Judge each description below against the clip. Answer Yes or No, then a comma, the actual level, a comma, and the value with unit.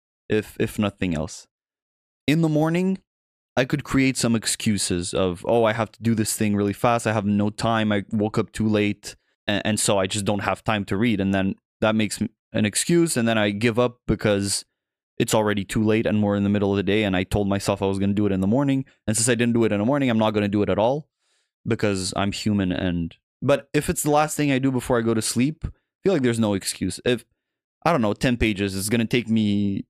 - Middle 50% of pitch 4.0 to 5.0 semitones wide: No, average, 3.0 semitones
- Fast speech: Yes, fast, 255 wpm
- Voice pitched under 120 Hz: Yes, low, 110 Hz